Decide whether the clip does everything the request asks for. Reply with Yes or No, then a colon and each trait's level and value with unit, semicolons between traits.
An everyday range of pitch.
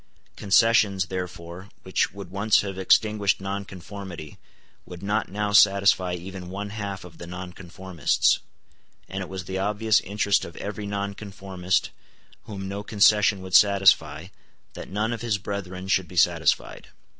No: narrow, 1.8 semitones